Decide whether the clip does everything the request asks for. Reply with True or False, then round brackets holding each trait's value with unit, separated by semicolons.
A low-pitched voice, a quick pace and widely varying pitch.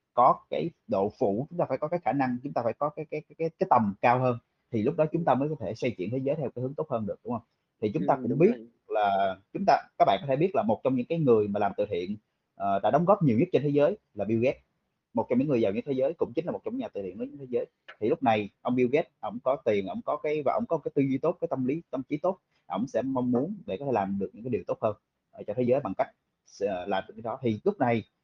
True (130 Hz; 320 wpm; 5.7 semitones)